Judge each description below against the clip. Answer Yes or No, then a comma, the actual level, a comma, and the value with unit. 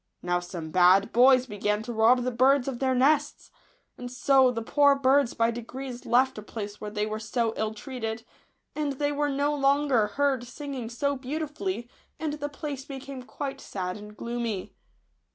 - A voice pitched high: Yes, very high, 250 Hz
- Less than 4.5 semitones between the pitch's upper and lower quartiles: Yes, average, 4.1 semitones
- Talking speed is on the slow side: No, average, 175 wpm